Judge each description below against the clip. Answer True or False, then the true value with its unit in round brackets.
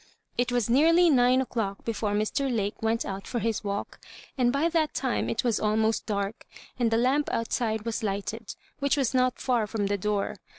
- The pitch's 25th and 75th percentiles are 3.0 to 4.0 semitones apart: True (3.3 semitones)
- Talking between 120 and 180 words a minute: False (195 wpm)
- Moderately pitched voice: False (230 Hz)